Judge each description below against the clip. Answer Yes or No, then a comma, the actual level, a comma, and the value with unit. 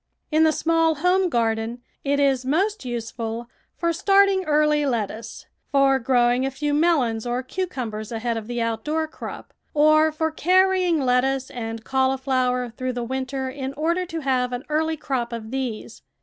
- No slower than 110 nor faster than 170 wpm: Yes, average, 160 wpm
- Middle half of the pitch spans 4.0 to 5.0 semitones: Yes, average, 4.5 semitones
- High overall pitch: Yes, very high, 265 Hz